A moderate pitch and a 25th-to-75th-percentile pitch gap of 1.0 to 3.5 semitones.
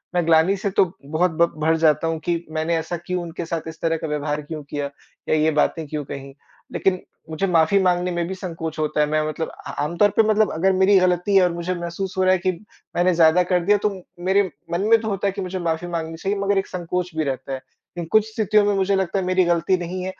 Yes: medium, 175 Hz; average, 2.9 semitones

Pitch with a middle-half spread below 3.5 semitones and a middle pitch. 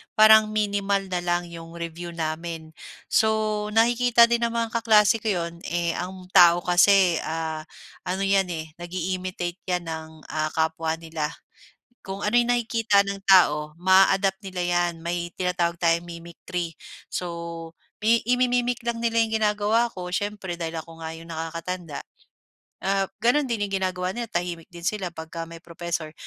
No: average, 3.8 semitones; medium, 180 Hz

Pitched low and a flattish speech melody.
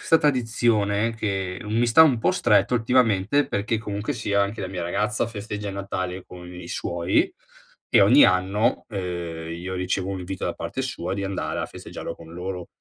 No: low, 100 Hz; average, 3.6 semitones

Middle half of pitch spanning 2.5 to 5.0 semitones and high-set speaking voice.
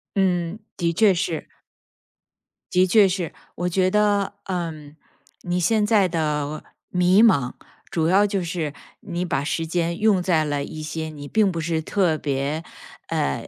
No: average, 3.5 semitones; medium, 175 Hz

